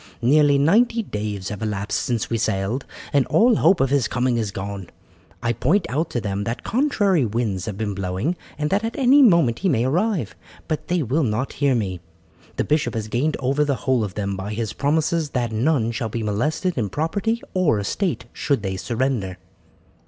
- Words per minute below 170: No, average, 195 wpm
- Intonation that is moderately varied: No, wide, 6.9 semitones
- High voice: No, low, 125 Hz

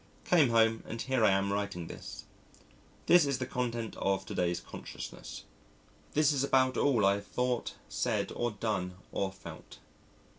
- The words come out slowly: No, average, 160 wpm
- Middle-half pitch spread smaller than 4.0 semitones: No, average, 4.8 semitones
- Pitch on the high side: No, low, 115 Hz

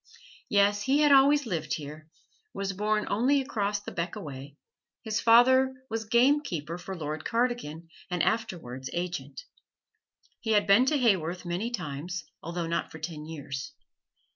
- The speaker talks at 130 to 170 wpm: Yes, average, 145 wpm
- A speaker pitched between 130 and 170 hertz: No, high, 195 Hz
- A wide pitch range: Yes, wide, 6.6 semitones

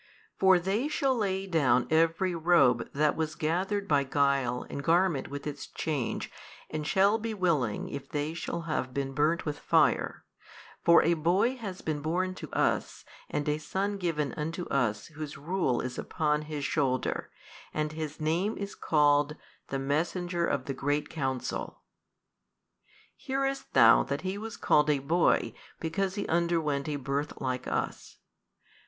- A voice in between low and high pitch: Yes, medium, 155 Hz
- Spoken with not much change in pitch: No, average, 4.3 semitones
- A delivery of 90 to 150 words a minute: No, average, 160 wpm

